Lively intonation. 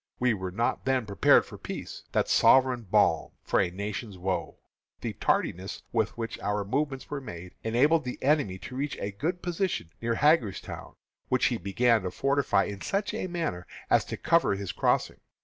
Yes: wide, 6.3 semitones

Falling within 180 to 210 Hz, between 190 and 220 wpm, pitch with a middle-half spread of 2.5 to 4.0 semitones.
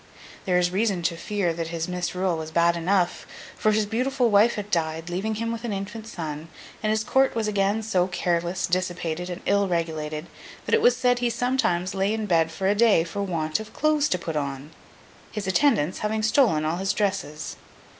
No: high, 190 Hz; average, 195 wpm; average, 4.4 semitones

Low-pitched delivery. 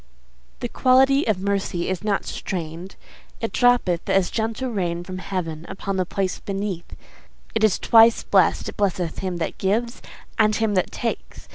No: high, 195 Hz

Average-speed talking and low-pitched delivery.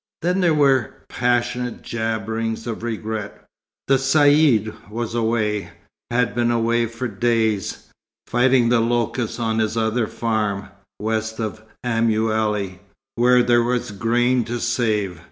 No: slow, 125 wpm; low, 115 Hz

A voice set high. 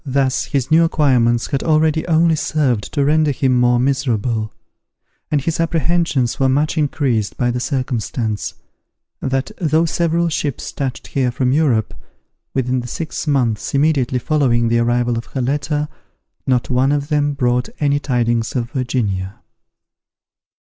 No: low, 135 Hz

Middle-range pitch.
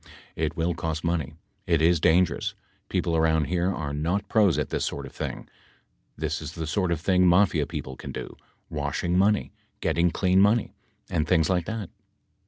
No: very low, 85 Hz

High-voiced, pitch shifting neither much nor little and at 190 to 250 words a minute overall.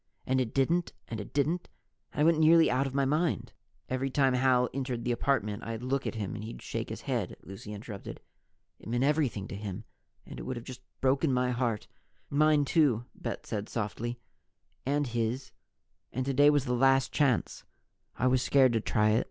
No: low, 130 Hz; average, 3.2 semitones; average, 200 wpm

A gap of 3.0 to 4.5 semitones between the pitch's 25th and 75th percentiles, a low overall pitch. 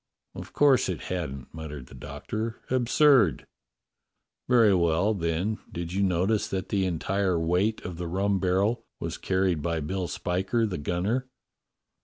Yes: average, 4.2 semitones; very low, 95 Hz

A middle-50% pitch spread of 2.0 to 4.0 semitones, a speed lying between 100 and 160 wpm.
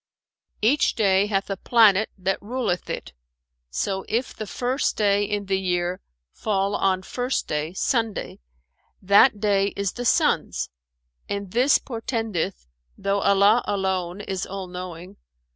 Yes: narrow, 2.6 semitones; slow, 135 wpm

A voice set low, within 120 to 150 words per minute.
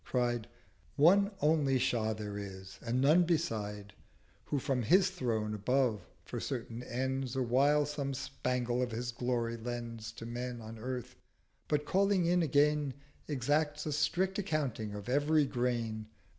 Yes: low, 125 Hz; average, 145 wpm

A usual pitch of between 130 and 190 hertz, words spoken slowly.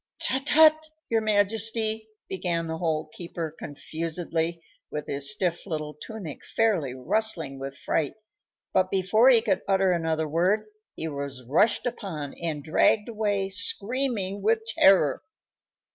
Yes: medium, 185 Hz; slow, 130 wpm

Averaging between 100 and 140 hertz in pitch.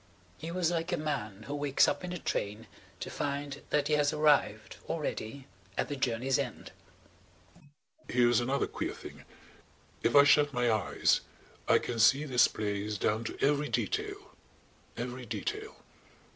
Yes: low, 135 Hz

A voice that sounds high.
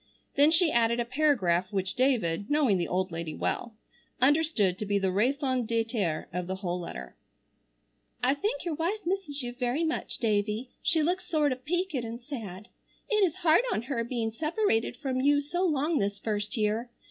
Yes: high, 245 Hz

